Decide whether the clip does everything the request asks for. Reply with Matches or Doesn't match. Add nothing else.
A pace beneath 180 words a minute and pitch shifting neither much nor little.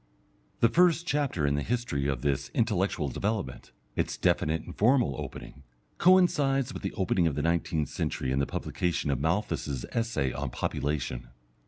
Doesn't match